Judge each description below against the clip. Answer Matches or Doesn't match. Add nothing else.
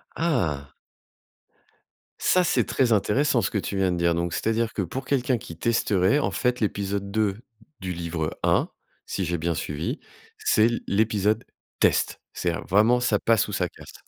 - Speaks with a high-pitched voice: Doesn't match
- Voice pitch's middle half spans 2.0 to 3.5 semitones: Doesn't match